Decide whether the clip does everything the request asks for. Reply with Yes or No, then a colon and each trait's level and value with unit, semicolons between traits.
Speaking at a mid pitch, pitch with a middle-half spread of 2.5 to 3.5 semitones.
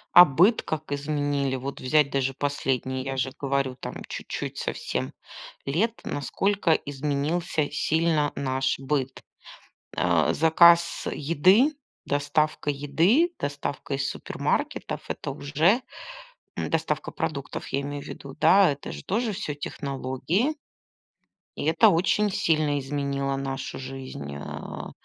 Yes: medium, 145 Hz; average, 3.2 semitones